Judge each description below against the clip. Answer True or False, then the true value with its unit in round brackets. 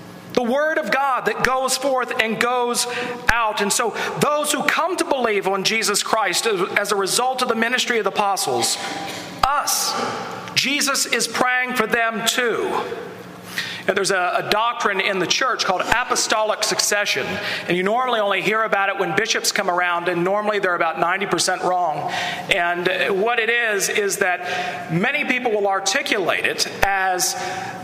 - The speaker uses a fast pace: False (165 wpm)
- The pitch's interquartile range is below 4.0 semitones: False (4.5 semitones)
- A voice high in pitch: True (215 Hz)